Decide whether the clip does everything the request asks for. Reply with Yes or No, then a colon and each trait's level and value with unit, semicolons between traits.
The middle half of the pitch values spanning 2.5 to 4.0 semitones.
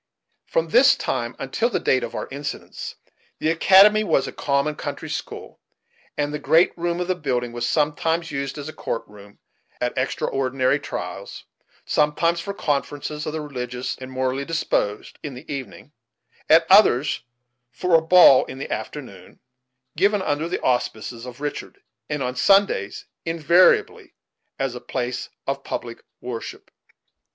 No: average, 4.5 semitones